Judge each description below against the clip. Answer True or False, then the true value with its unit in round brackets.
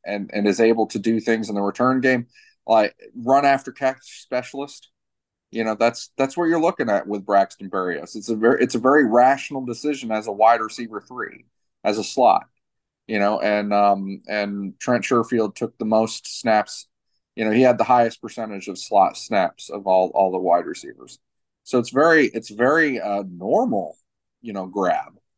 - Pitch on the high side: False (115 Hz)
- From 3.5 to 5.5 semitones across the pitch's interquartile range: True (3.8 semitones)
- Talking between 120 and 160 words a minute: False (190 wpm)